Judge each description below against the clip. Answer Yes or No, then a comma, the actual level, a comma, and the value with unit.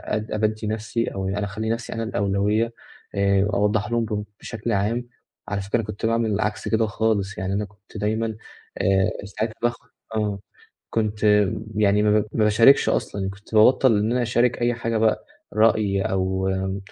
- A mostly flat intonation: Yes, narrow, 2.0 semitones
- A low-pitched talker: Yes, low, 105 Hz